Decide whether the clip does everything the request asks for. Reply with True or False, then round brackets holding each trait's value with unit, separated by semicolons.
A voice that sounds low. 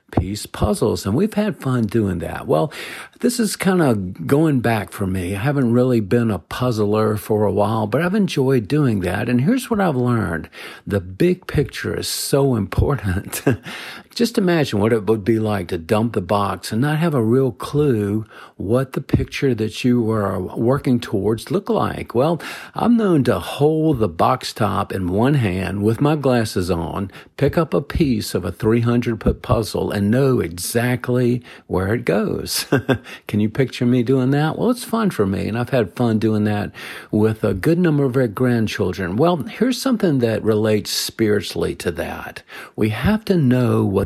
True (120 Hz)